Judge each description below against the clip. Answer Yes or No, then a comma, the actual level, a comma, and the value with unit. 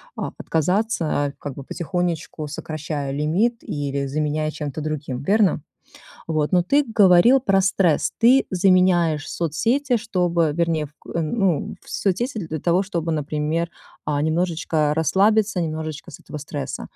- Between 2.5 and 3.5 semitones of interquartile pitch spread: No, average, 4.1 semitones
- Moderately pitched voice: Yes, medium, 165 Hz